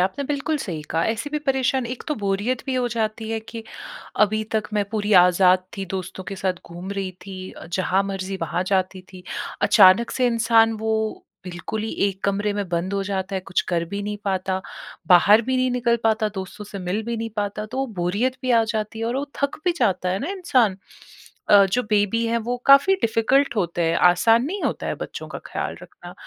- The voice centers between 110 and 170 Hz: No, high, 210 Hz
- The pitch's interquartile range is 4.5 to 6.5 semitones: No, average, 3.8 semitones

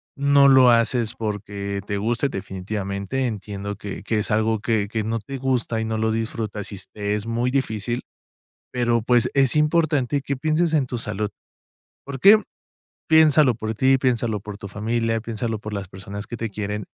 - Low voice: Yes, low, 115 Hz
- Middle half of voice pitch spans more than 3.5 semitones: Yes, average, 3.9 semitones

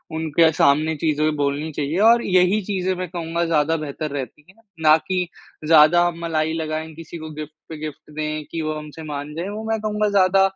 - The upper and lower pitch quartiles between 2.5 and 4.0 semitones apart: Yes, average, 2.8 semitones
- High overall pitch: No, medium, 160 Hz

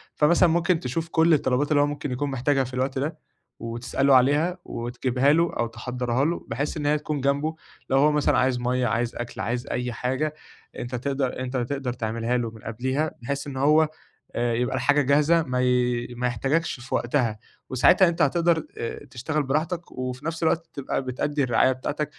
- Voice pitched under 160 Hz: Yes, low, 135 Hz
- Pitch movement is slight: No, average, 3.4 semitones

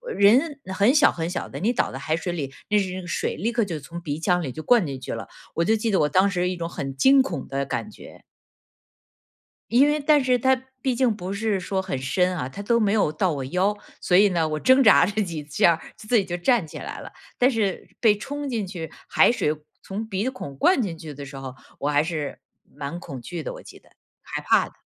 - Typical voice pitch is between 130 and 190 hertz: Yes, medium, 185 Hz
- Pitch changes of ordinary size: No, wide, 6.2 semitones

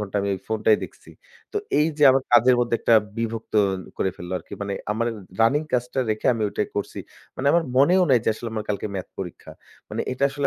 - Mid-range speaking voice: No, low, 115 Hz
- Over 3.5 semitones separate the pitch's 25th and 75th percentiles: Yes, average, 4.1 semitones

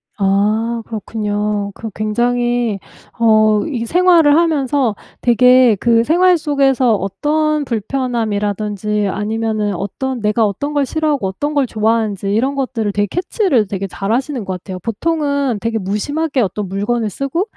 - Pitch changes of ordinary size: Yes, average, 5.0 semitones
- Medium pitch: No, high, 230 Hz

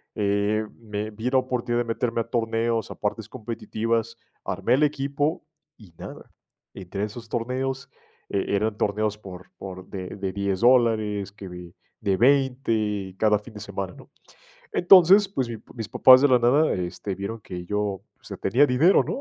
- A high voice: No, low, 110 Hz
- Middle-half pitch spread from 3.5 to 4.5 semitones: Yes, average, 3.9 semitones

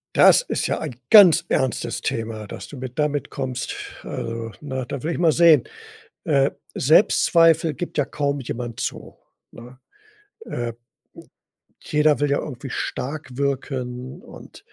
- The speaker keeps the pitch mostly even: No, average, 3.6 semitones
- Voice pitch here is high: No, medium, 140 Hz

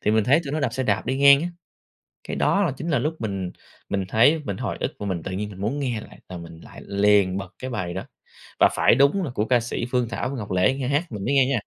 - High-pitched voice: No, low, 120 Hz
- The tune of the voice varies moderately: No, wide, 5.7 semitones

